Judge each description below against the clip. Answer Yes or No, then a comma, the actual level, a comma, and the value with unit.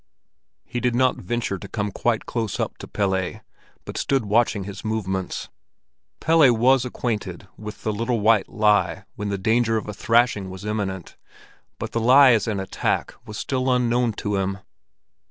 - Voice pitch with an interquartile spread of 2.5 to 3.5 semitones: Yes, average, 3.1 semitones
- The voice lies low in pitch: Yes, low, 110 Hz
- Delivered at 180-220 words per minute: No, average, 170 wpm